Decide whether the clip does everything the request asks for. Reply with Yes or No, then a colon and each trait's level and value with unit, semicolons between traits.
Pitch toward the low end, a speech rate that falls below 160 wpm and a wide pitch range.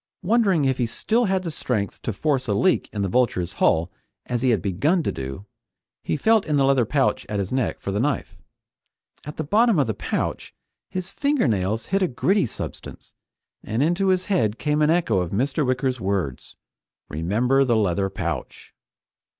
No: low, 130 Hz; average, 185 wpm; wide, 8.4 semitones